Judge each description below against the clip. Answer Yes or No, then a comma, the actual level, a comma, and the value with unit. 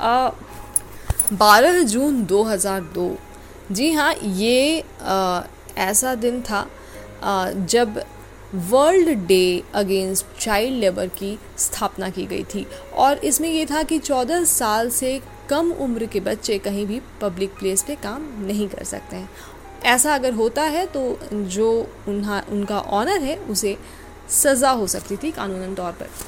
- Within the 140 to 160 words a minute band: Yes, average, 145 wpm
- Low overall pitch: No, high, 210 Hz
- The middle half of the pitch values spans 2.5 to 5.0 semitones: No, wide, 5.5 semitones